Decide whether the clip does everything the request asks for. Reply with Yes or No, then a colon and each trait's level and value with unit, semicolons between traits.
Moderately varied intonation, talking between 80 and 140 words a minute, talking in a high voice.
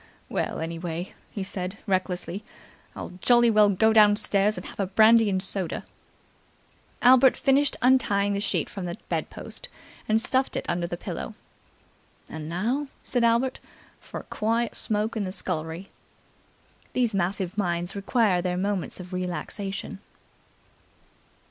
Yes: average, 3.7 semitones; slow, 135 wpm; high, 200 Hz